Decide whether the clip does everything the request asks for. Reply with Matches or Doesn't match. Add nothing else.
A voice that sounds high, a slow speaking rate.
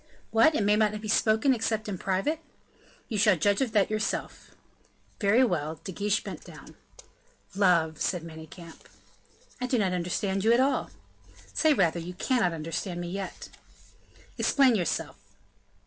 Doesn't match